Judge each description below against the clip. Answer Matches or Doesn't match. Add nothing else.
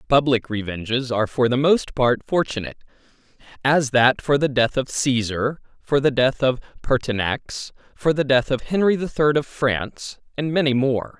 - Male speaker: Matches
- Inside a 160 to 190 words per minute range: Matches